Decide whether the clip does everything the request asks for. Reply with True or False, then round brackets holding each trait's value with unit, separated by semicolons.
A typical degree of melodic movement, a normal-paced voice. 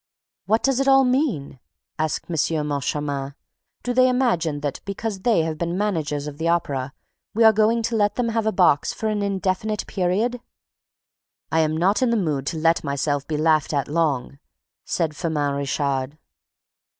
False (6.9 semitones; 175 wpm)